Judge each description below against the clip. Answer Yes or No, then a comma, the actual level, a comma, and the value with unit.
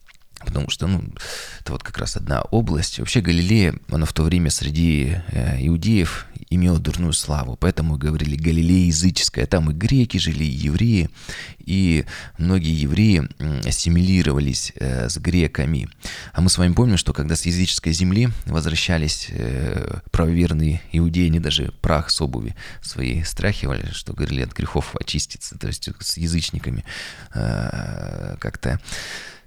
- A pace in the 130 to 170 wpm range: Yes, average, 135 wpm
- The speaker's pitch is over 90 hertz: No, very low, 85 Hz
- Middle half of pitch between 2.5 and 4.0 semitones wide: Yes, average, 3.0 semitones